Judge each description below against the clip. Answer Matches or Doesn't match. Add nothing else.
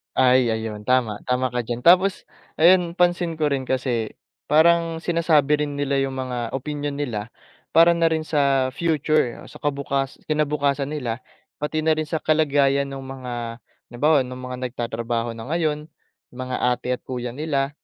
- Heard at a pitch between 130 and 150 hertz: Matches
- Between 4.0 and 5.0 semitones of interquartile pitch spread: Doesn't match